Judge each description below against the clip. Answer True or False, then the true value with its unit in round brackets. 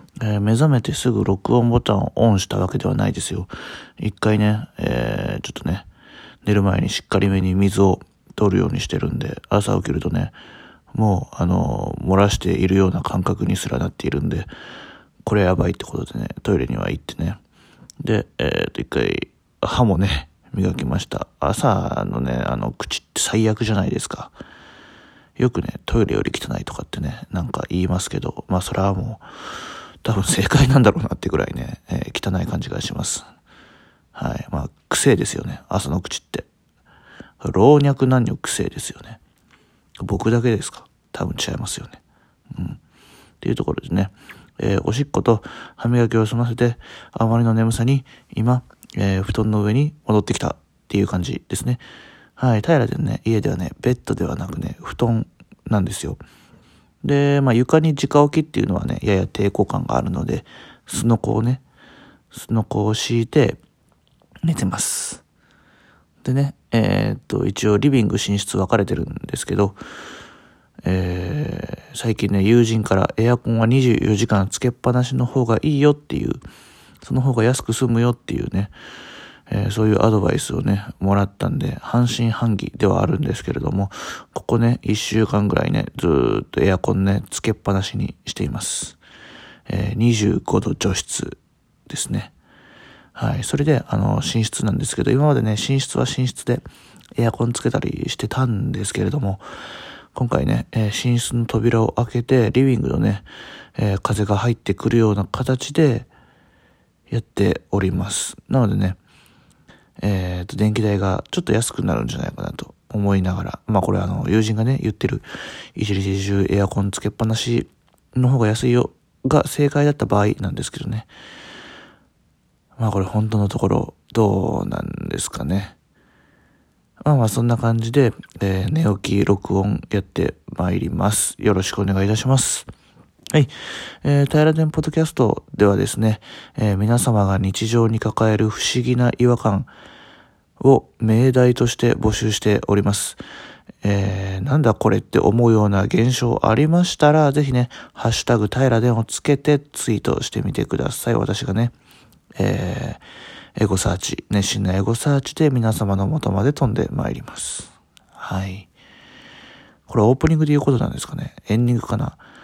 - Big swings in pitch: False (3.9 semitones)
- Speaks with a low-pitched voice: True (110 Hz)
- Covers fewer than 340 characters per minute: True (325 characters per minute)